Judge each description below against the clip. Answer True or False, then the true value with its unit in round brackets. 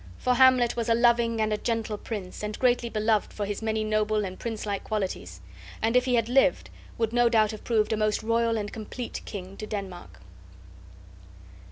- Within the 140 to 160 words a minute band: False (190 wpm)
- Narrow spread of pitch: True (1.9 semitones)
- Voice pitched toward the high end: True (220 Hz)